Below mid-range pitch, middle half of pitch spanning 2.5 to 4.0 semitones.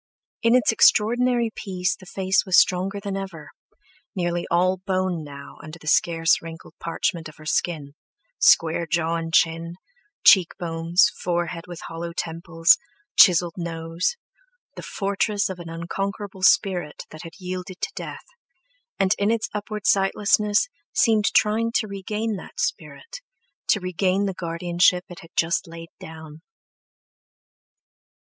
No: medium, 180 Hz; average, 3.4 semitones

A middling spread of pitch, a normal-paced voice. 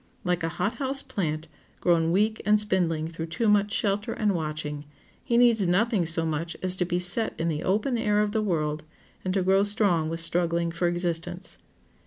Yes: average, 4.0 semitones; average, 195 wpm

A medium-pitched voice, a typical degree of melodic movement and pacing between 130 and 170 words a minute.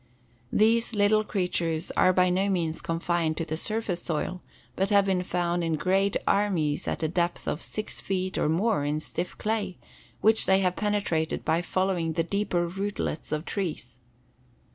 Yes: medium, 180 Hz; average, 3.3 semitones; average, 165 wpm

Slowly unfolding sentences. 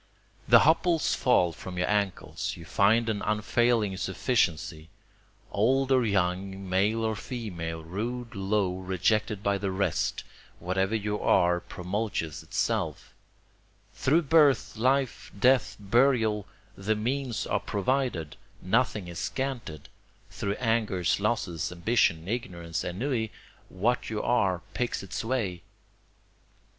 Yes: slow, 115 wpm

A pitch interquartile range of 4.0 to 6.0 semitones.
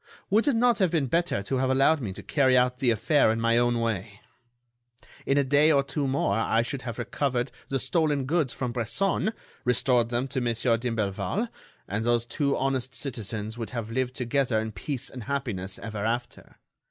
No: average, 3.4 semitones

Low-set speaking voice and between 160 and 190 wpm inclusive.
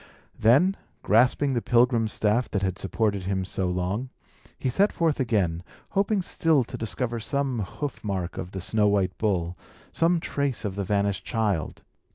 Yes: low, 110 Hz; average, 165 wpm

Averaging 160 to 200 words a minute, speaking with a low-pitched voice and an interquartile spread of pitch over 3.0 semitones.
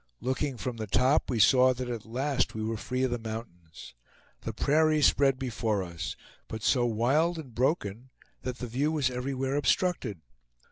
Yes: average, 175 wpm; low, 125 Hz; average, 3.4 semitones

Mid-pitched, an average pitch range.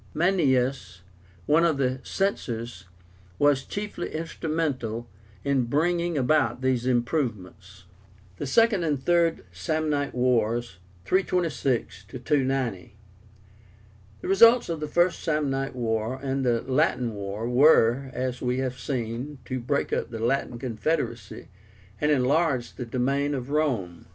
No: low, 130 Hz; average, 4.4 semitones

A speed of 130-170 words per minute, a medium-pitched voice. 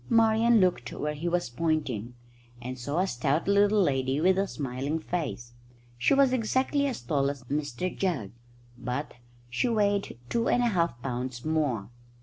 Yes: average, 160 wpm; medium, 155 Hz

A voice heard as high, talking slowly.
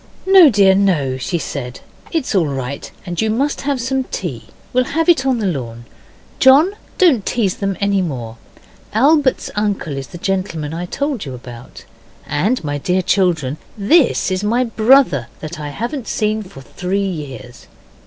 No: high, 195 Hz; average, 165 wpm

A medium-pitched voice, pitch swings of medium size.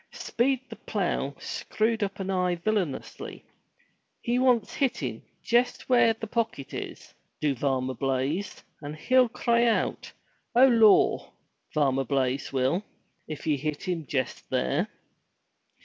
No: medium, 180 Hz; wide, 9.0 semitones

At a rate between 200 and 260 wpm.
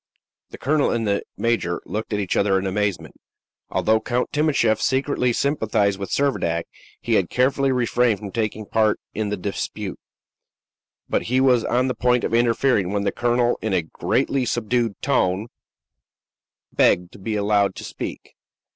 No: average, 160 wpm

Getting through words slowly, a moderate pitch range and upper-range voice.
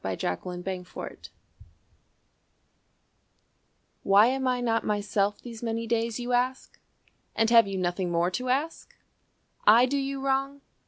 Yes: slow, 130 wpm; average, 4.5 semitones; high, 230 Hz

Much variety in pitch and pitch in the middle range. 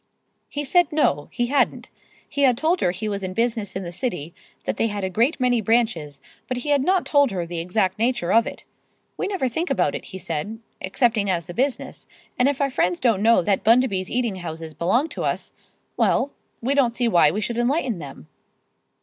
No: wide, 5.8 semitones; high, 225 Hz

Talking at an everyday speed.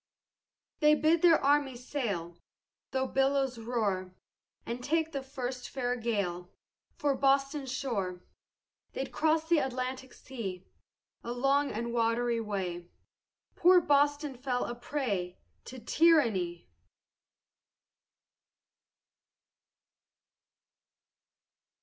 No: slow, 95 wpm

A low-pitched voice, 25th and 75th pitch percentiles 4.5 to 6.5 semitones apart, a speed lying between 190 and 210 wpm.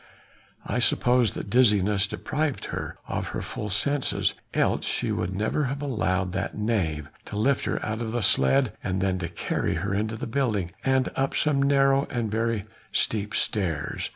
No: low, 110 Hz; average, 5.2 semitones; average, 175 wpm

